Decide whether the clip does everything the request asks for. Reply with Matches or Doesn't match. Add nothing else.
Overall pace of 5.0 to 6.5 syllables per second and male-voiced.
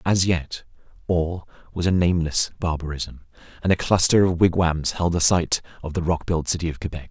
Matches